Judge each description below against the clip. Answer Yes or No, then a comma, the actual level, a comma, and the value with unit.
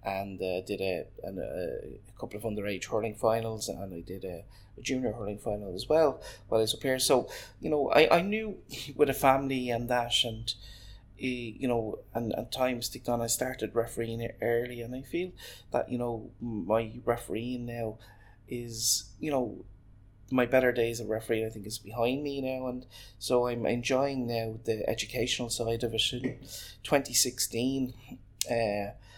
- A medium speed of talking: Yes, average, 175 wpm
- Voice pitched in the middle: No, low, 115 Hz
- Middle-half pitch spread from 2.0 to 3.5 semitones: Yes, average, 2.8 semitones